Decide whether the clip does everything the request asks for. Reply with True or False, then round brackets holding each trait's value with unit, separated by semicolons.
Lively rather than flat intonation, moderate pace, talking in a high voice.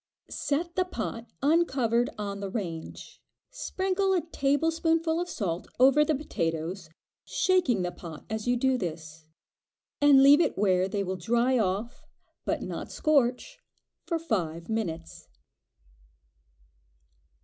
False (8.7 semitones; 125 wpm; 240 Hz)